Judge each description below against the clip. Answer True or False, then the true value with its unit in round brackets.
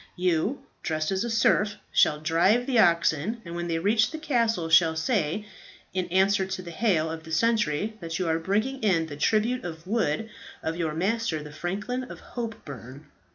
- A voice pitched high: False (180 Hz)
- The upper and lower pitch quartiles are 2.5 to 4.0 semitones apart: False (5.4 semitones)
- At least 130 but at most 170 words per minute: False (185 wpm)